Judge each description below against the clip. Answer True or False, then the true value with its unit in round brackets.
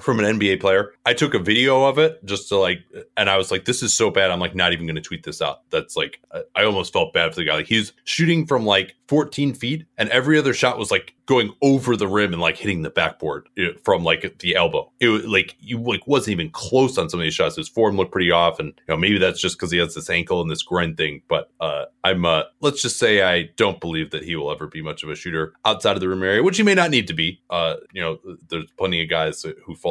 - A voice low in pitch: True (110 Hz)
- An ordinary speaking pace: False (275 wpm)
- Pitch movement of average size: False (7.4 semitones)